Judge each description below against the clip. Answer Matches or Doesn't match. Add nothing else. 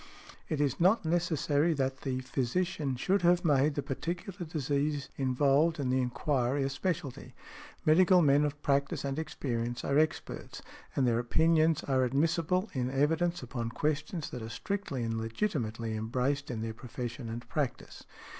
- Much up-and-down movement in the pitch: Doesn't match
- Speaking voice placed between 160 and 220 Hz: Doesn't match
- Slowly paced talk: Doesn't match